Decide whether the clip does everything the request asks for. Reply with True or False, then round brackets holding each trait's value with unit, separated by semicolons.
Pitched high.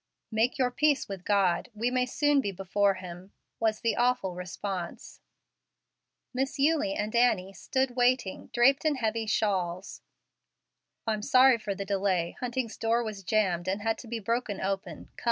True (220 Hz)